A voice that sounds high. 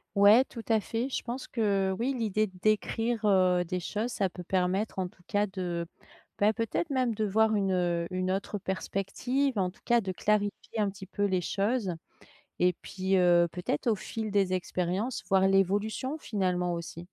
Yes: high, 195 Hz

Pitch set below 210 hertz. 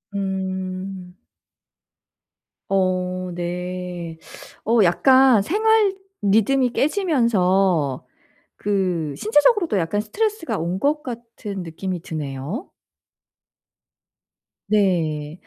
Yes: high, 190 Hz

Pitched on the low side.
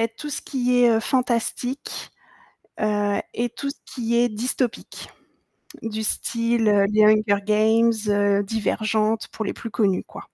No: high, 225 Hz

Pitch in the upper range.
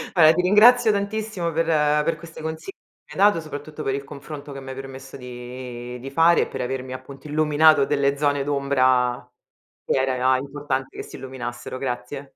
No: medium, 140 Hz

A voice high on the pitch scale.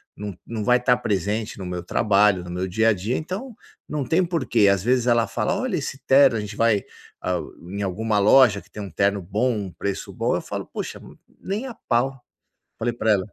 No: low, 110 Hz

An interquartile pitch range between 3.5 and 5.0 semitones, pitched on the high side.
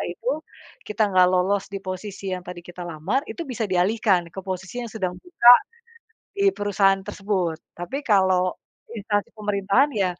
No: average, 2.8 semitones; high, 195 Hz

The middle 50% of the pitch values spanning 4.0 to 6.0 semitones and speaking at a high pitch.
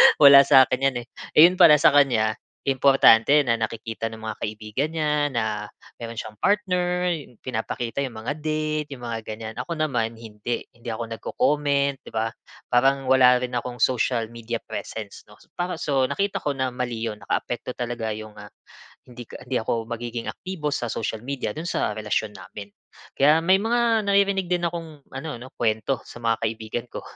No: average, 4.9 semitones; low, 125 Hz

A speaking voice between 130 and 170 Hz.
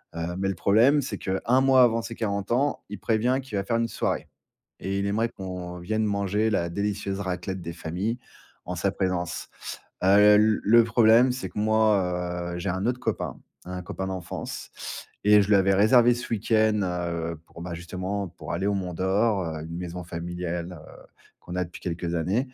No: low, 100 Hz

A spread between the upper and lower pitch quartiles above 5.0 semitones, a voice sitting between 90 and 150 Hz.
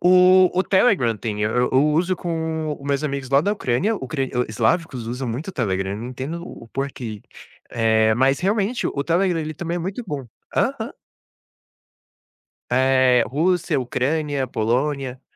Yes: wide, 5.6 semitones; medium, 140 Hz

